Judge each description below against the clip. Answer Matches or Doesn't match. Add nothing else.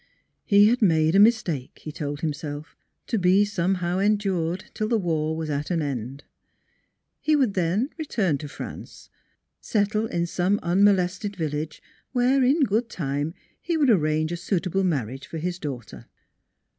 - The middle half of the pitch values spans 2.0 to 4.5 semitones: Doesn't match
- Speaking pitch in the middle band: Matches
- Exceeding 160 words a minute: Doesn't match